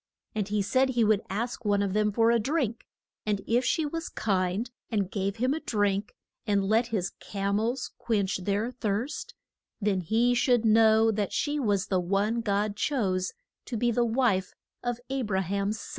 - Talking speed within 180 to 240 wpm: Yes, average, 190 wpm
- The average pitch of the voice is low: No, high, 215 Hz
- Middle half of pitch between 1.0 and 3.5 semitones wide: Yes, average, 3.1 semitones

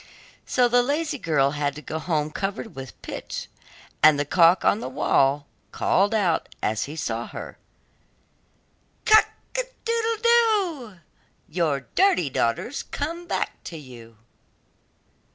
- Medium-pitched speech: Yes, medium, 175 Hz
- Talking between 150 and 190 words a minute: No, slow, 135 wpm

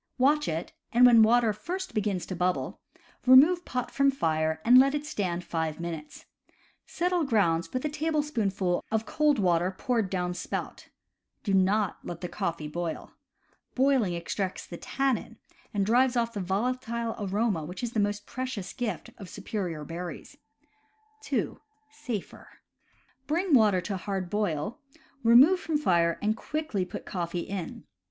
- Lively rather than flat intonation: Yes, wide, 6.3 semitones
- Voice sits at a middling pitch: No, high, 210 Hz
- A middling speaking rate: Yes, average, 150 wpm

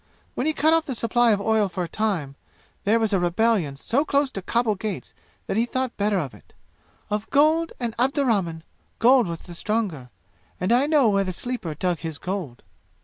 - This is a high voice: Yes, high, 215 Hz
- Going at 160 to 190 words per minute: No, average, 200 wpm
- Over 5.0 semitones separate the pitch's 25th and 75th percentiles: Yes, wide, 5.6 semitones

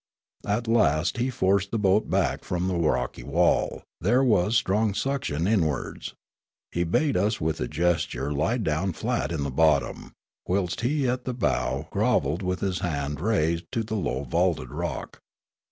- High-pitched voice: No, very low, 90 Hz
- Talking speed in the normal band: Yes, average, 170 wpm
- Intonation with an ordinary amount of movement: No, wide, 6.0 semitones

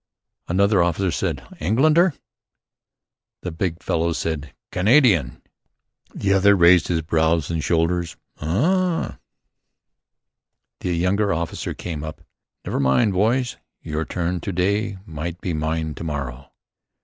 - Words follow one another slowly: Yes, slow, 120 wpm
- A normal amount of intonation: Yes, average, 3.8 semitones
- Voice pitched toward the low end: Yes, very low, 85 Hz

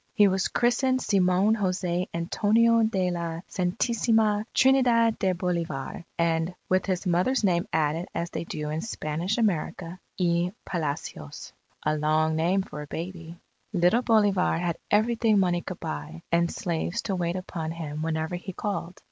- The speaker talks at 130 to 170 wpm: Yes, average, 150 wpm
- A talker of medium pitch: Yes, medium, 180 Hz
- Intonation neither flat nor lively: Yes, average, 3.8 semitones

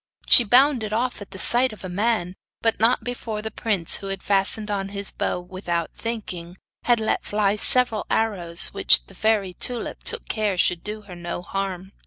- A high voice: Yes, high, 205 Hz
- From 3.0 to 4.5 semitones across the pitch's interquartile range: Yes, average, 3.3 semitones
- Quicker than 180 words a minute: Yes, average, 190 wpm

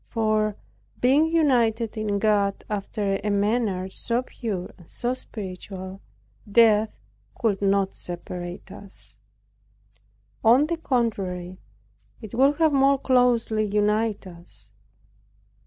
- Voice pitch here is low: No, high, 215 Hz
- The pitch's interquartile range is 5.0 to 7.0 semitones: No, average, 3.7 semitones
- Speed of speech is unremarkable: No, slow, 105 wpm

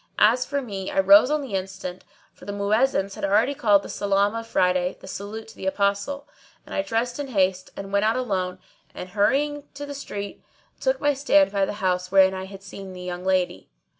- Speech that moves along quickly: Yes, fast, 215 wpm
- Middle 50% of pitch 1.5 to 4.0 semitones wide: No, average, 4.7 semitones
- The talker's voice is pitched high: Yes, high, 200 Hz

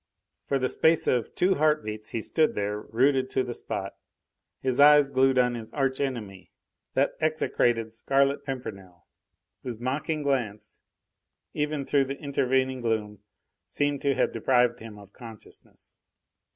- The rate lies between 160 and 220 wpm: No, average, 145 wpm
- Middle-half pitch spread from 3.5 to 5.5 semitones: Yes, average, 3.8 semitones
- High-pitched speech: No, low, 130 Hz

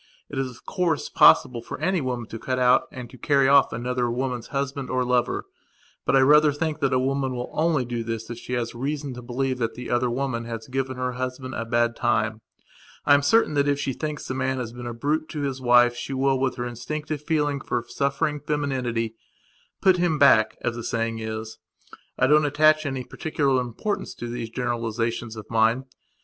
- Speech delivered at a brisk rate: Yes, fast, 210 wpm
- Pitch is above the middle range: No, low, 130 Hz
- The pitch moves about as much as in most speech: Yes, average, 3.0 semitones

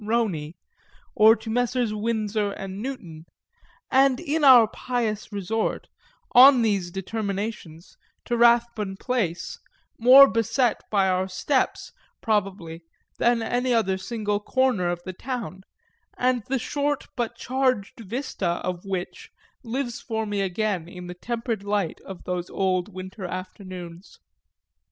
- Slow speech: Yes, slow, 130 wpm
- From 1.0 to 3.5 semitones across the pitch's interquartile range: No, average, 4.4 semitones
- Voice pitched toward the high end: Yes, high, 215 Hz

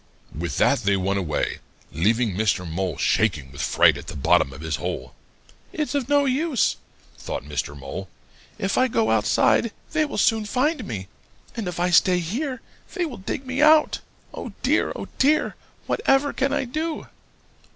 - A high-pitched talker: Yes, high, 195 Hz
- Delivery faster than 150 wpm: Yes, average, 175 wpm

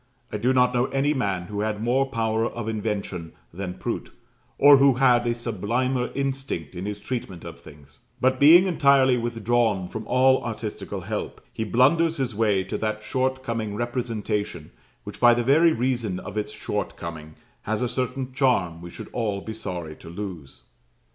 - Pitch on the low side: Yes, low, 115 Hz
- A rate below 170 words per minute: No, average, 175 wpm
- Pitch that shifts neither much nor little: Yes, average, 4.2 semitones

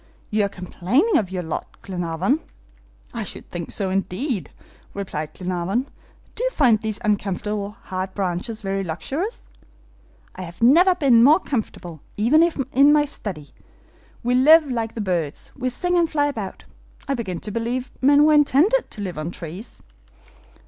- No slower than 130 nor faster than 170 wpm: Yes, average, 155 wpm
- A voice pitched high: Yes, high, 220 Hz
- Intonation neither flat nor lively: No, wide, 7.1 semitones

